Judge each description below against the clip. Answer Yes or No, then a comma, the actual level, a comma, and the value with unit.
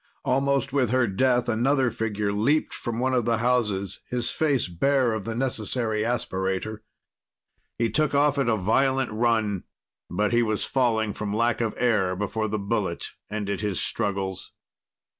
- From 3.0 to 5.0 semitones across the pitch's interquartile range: Yes, average, 3.5 semitones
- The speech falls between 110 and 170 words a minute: Yes, average, 160 wpm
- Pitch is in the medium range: No, low, 115 Hz